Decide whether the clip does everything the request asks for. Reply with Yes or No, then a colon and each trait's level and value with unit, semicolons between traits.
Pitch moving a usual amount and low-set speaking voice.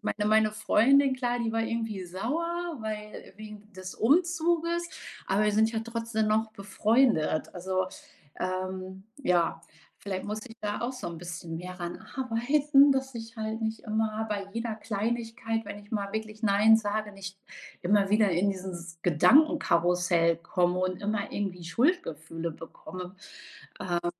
No: average, 3.7 semitones; high, 210 Hz